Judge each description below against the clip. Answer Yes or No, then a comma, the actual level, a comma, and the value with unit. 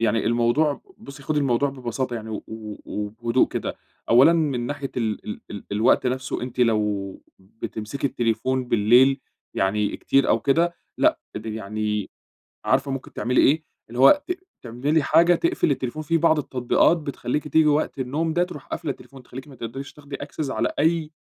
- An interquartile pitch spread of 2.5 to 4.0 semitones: No, average, 4.5 semitones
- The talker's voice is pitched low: Yes, low, 130 Hz